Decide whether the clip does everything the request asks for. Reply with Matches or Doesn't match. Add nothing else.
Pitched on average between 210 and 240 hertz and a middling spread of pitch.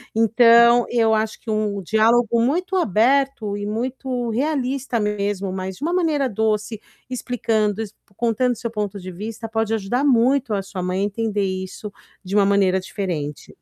Matches